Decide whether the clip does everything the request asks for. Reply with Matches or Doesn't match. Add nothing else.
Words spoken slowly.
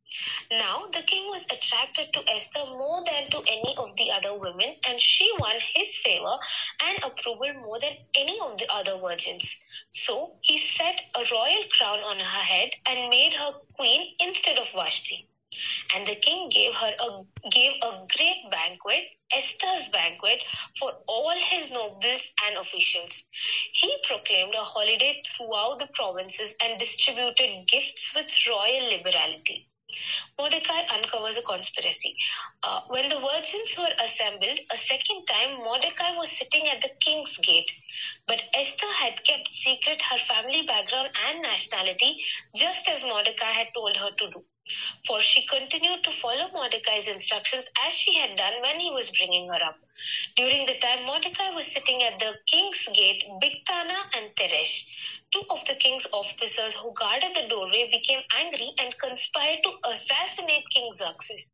Doesn't match